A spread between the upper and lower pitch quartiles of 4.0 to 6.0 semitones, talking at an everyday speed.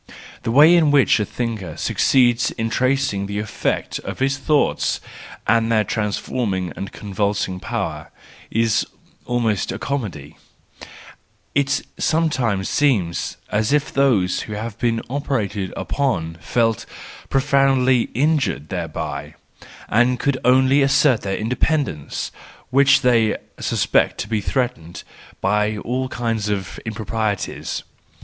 No: average, 4.7 semitones; slow, 125 wpm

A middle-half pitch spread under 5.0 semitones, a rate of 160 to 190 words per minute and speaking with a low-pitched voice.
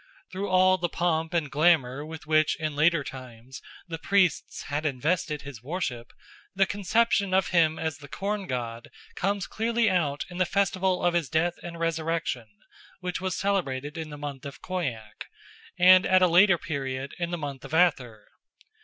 No: average, 4.5 semitones; average, 170 wpm; medium, 165 Hz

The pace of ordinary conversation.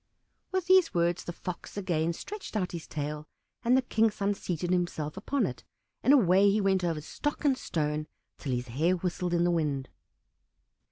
Yes: average, 180 wpm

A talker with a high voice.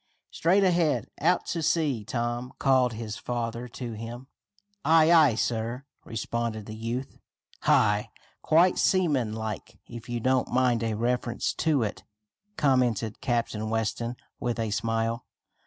No: low, 120 Hz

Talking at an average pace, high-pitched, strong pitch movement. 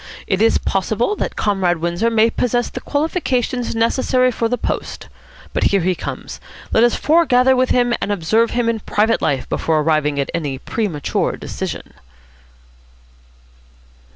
Yes: average, 150 wpm; high, 225 Hz; wide, 5.9 semitones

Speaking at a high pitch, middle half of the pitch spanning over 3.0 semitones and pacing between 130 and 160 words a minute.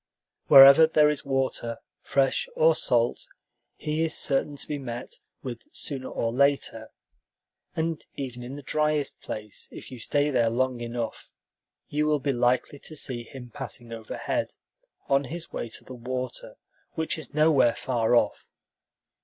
No: low, 135 Hz; average, 3.7 semitones; average, 155 wpm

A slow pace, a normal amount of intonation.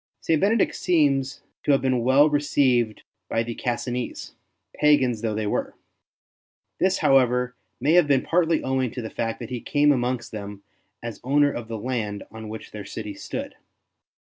No: average, 170 wpm; average, 4.2 semitones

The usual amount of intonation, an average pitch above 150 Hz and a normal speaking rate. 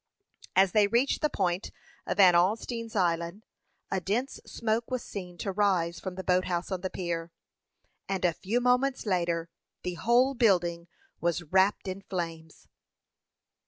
Yes: average, 4.1 semitones; high, 190 Hz; average, 155 wpm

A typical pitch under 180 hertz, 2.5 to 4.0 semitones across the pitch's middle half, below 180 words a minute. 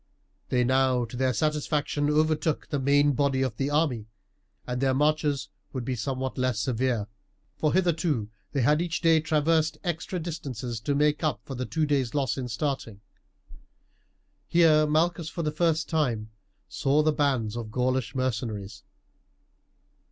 Yes: medium, 140 Hz; average, 3.5 semitones; average, 150 wpm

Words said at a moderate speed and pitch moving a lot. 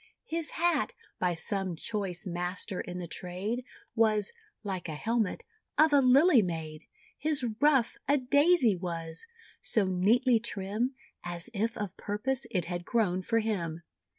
Yes: average, 145 wpm; wide, 5.9 semitones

